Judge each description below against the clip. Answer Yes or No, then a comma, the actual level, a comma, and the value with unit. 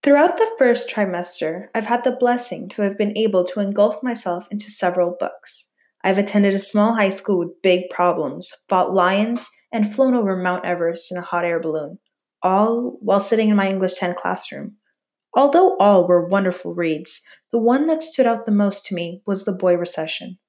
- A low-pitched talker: No, high, 200 Hz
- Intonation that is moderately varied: Yes, average, 4.1 semitones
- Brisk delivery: No, average, 190 wpm